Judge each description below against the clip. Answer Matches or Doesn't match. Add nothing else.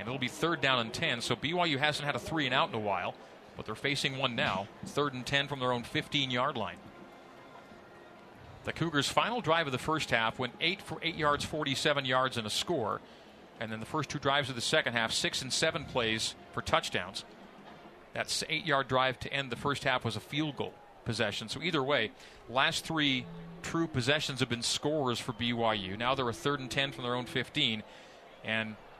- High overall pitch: Doesn't match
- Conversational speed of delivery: Doesn't match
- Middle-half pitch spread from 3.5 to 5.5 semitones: Matches